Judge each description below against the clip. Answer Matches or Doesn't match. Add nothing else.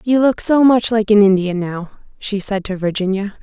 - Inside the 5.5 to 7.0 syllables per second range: Doesn't match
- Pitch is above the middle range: Matches